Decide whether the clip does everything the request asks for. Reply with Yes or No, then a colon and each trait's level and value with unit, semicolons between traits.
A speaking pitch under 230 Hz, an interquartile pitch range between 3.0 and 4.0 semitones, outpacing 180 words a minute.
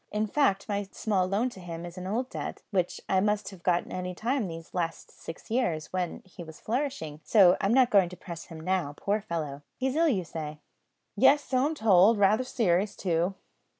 No: high, 190 Hz; average, 4.4 semitones; fast, 205 wpm